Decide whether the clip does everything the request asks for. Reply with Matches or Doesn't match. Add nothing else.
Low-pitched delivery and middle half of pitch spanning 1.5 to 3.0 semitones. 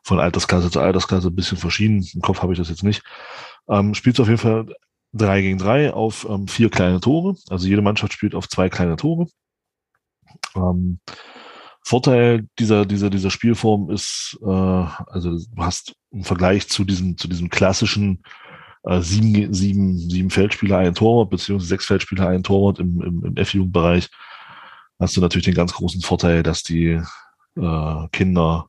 Matches